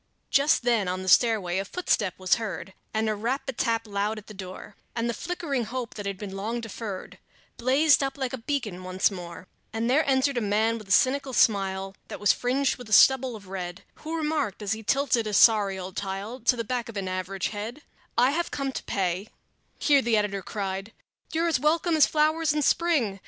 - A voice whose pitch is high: Yes, high, 225 Hz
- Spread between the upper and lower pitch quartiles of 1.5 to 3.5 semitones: No, average, 5.3 semitones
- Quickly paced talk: Yes, fast, 215 wpm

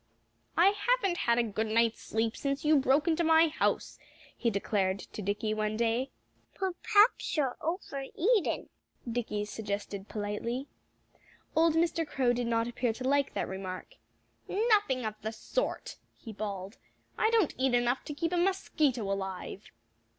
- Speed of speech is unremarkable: Yes, average, 150 wpm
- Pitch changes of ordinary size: No, wide, 7.1 semitones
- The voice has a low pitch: No, high, 245 Hz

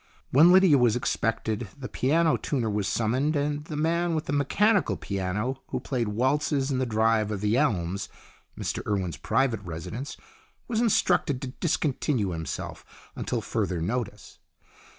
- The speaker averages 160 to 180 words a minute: No, average, 150 wpm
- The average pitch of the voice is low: Yes, low, 125 Hz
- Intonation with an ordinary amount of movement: No, wide, 5.9 semitones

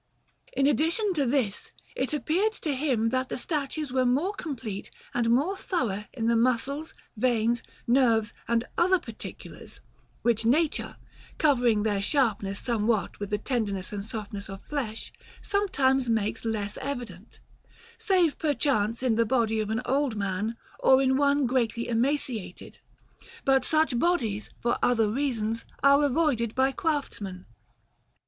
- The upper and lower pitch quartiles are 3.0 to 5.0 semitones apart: Yes, average, 4.4 semitones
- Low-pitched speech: No, high, 245 Hz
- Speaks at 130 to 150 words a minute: Yes, average, 140 wpm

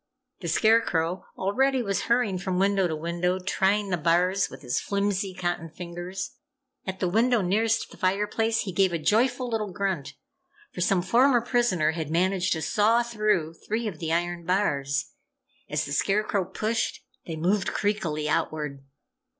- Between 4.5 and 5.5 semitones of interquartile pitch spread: No, average, 3.8 semitones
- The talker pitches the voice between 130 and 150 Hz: No, high, 190 Hz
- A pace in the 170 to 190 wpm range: No, average, 160 wpm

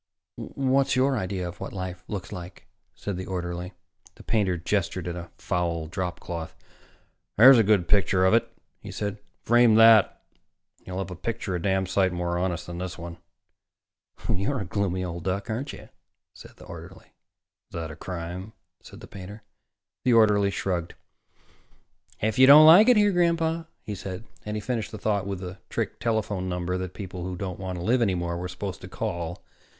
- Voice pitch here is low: Yes, very low, 95 Hz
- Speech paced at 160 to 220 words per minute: Yes, average, 190 wpm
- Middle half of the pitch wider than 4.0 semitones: No, average, 3.6 semitones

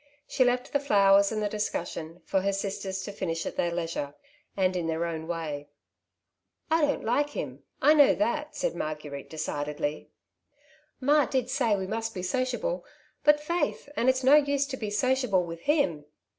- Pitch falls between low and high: No, high, 205 Hz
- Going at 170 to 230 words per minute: Yes, average, 185 wpm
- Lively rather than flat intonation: Yes, wide, 8.7 semitones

